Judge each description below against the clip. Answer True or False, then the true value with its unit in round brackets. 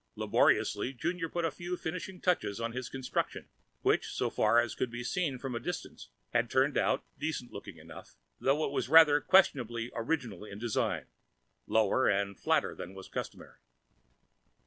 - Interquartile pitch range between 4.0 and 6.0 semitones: True (5.6 semitones)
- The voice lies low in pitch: True (130 Hz)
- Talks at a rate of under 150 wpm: False (165 wpm)